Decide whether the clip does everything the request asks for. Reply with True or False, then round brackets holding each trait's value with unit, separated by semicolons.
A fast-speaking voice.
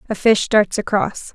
False (180 wpm)